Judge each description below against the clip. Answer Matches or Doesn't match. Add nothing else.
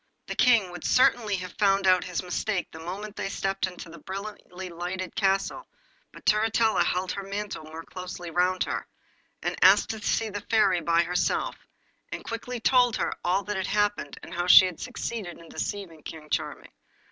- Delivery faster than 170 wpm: Matches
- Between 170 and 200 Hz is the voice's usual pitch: Matches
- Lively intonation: Doesn't match